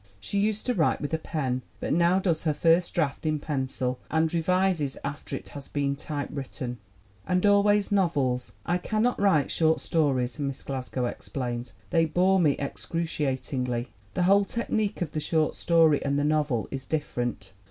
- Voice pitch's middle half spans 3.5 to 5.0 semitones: Yes, average, 4.6 semitones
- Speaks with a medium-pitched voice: Yes, medium, 155 Hz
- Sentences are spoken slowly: No, average, 170 wpm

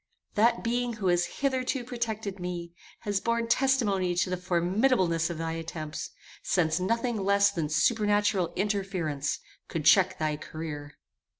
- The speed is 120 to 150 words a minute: Yes, slow, 135 wpm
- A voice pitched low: No, high, 190 Hz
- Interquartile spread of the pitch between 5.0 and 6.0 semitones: Yes, wide, 5.4 semitones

